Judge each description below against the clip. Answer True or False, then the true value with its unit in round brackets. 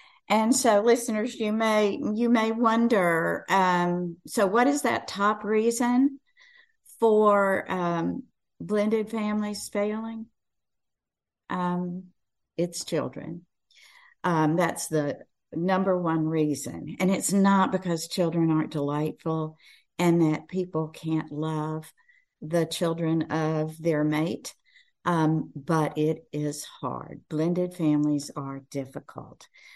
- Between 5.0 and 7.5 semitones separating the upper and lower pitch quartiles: True (5.6 semitones)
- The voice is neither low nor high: True (180 Hz)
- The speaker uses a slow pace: True (110 wpm)